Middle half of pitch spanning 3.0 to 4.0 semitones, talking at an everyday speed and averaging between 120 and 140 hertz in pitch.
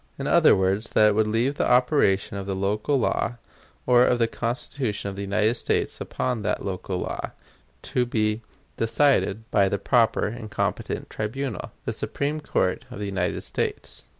No: average, 3.7 semitones; average, 175 wpm; low, 110 Hz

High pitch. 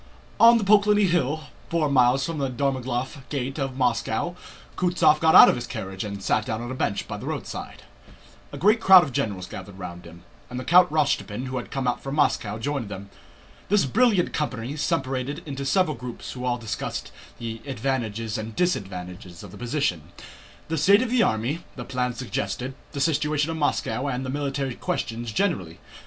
No: low, 130 Hz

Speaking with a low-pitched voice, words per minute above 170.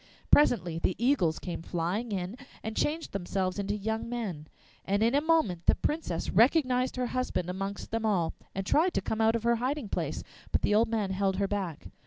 No: high, 210 Hz; average, 200 wpm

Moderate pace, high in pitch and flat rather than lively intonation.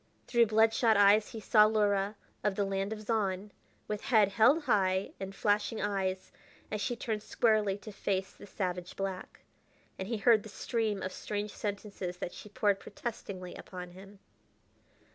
Yes: average, 165 wpm; high, 205 Hz; narrow, 2.0 semitones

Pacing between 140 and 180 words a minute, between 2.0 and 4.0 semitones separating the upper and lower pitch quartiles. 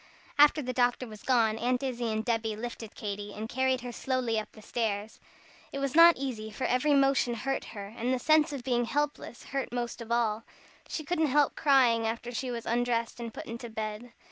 No: average, 200 wpm; average, 2.9 semitones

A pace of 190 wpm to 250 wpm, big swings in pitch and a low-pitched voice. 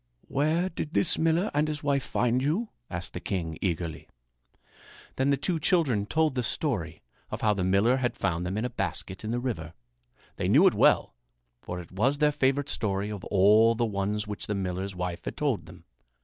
Yes: average, 200 wpm; wide, 7.1 semitones; low, 110 Hz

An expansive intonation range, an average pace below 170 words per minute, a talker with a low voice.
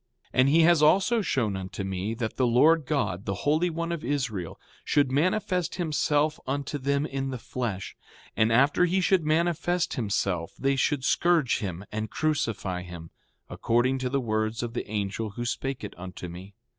No: wide, 6.6 semitones; average, 175 wpm; low, 130 Hz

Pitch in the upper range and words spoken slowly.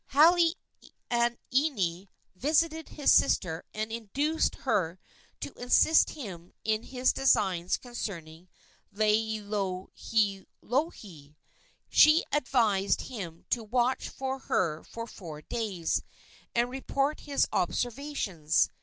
Yes: high, 225 Hz; slow, 90 wpm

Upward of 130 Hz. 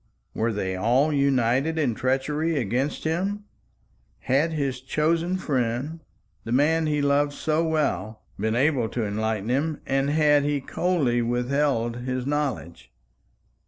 Yes: medium, 140 Hz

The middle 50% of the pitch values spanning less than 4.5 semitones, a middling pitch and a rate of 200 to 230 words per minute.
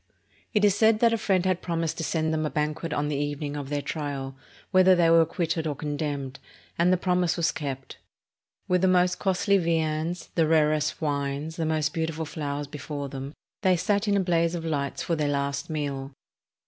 Yes: average, 3.5 semitones; medium, 160 Hz; fast, 205 wpm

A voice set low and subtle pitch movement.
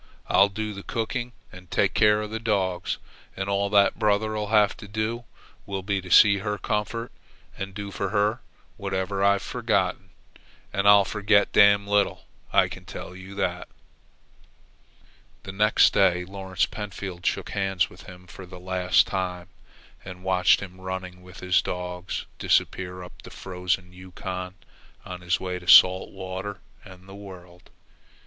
Yes: very low, 95 Hz; narrow, 1.9 semitones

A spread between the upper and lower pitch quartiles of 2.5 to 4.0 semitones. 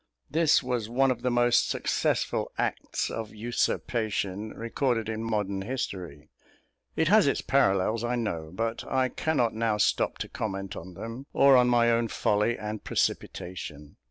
Yes: average, 3.2 semitones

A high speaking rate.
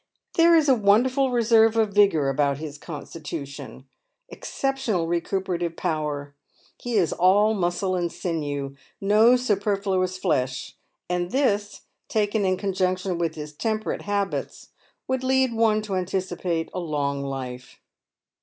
No: slow, 135 wpm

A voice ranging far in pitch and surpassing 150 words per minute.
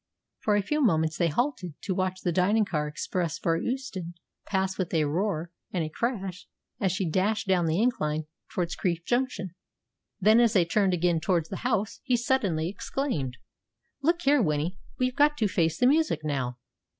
Yes: wide, 5.9 semitones; average, 180 wpm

